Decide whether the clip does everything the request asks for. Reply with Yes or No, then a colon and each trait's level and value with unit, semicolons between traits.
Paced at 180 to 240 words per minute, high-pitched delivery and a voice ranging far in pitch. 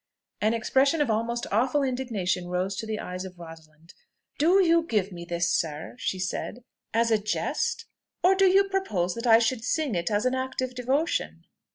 Yes: average, 190 wpm; high, 230 Hz; wide, 6.7 semitones